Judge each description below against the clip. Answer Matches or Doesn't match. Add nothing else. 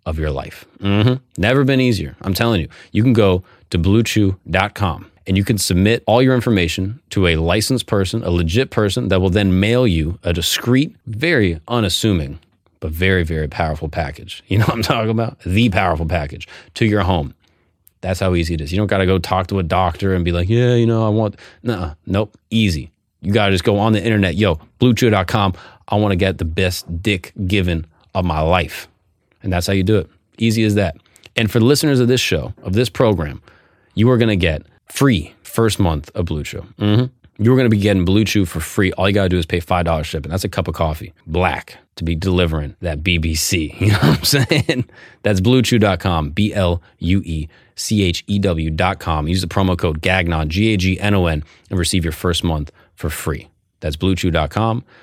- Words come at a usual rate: Doesn't match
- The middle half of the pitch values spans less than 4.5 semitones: Matches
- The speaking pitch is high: Doesn't match